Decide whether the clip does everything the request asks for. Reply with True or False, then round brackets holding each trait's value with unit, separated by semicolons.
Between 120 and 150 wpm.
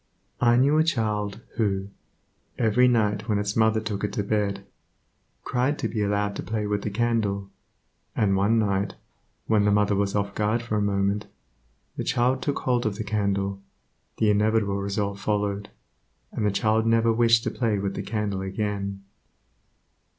False (170 wpm)